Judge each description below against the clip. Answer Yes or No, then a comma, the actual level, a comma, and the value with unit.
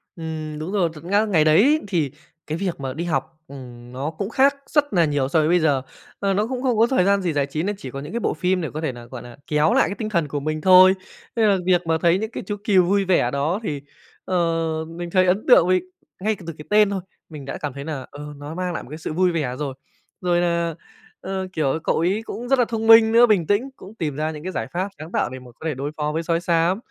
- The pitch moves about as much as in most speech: Yes, average, 4.8 semitones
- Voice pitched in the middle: Yes, medium, 170 Hz